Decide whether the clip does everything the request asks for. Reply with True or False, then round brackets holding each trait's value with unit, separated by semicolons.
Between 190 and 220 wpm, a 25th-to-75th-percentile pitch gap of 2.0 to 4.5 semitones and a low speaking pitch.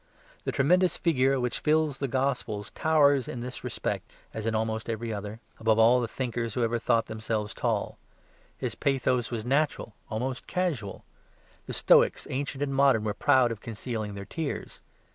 False (160 wpm; 3.7 semitones; 120 Hz)